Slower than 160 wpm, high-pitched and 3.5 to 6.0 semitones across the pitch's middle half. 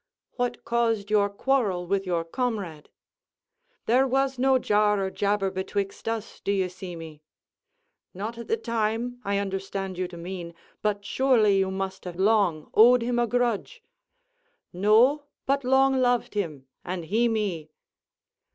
Yes: average, 145 wpm; high, 205 Hz; average, 4.2 semitones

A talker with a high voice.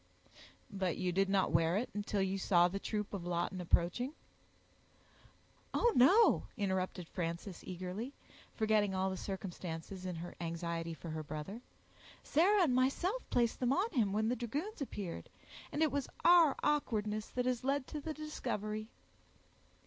Yes: high, 205 Hz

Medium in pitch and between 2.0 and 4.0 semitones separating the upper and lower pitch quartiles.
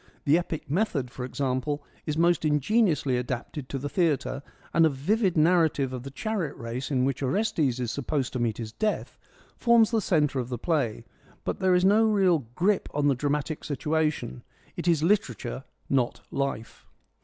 No: medium, 145 Hz; average, 5.1 semitones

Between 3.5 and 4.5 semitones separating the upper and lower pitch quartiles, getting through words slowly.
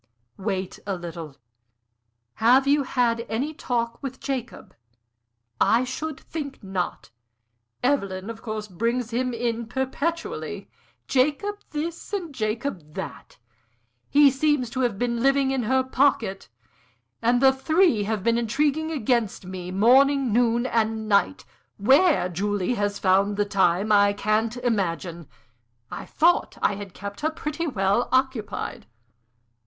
No: average, 5.0 semitones; slow, 130 wpm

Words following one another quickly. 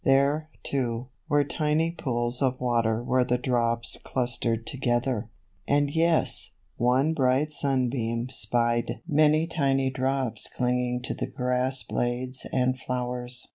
No: average, 145 wpm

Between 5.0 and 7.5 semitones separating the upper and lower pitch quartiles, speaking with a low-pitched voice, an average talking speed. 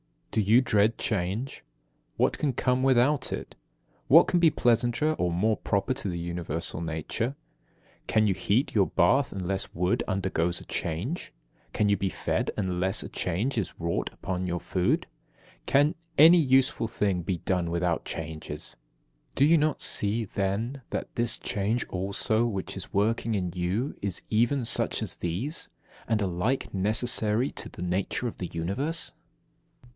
Yes: wide, 5.5 semitones; low, 105 Hz; average, 155 wpm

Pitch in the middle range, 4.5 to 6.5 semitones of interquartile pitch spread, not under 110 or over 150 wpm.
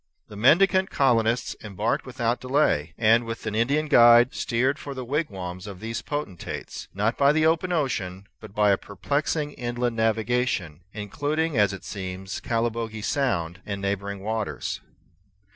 No: low, 115 Hz; average, 4.9 semitones; average, 145 wpm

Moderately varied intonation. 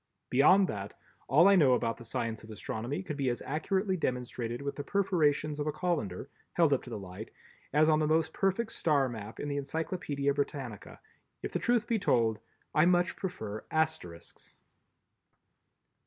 No: wide, 6.0 semitones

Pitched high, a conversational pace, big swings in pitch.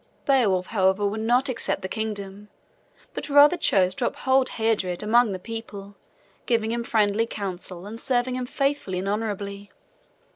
No: high, 220 Hz; average, 150 wpm; average, 3.5 semitones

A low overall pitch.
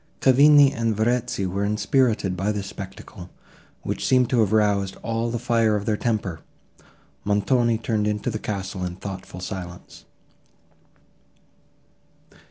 Yes: low, 105 Hz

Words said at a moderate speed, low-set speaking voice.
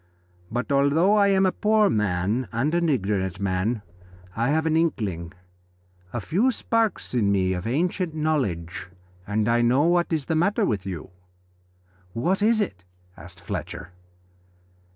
Yes: average, 150 wpm; low, 125 Hz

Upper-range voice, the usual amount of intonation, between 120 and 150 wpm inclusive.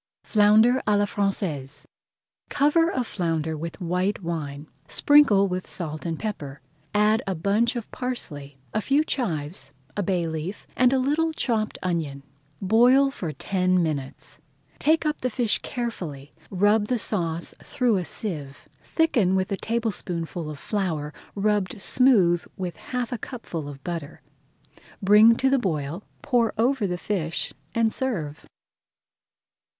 No: high, 195 Hz; wide, 6.2 semitones; average, 140 wpm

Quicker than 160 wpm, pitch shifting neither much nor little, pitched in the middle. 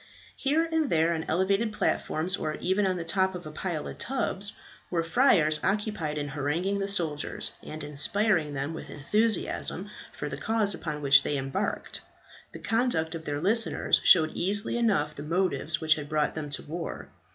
Yes: average, 185 wpm; average, 4.9 semitones; medium, 170 Hz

